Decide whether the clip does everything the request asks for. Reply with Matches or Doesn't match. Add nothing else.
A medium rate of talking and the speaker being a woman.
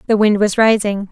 Doesn't match